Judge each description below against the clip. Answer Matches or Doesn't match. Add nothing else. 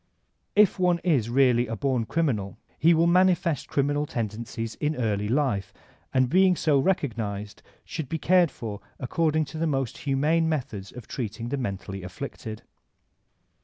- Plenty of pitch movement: Matches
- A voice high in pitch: Doesn't match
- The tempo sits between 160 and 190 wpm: Doesn't match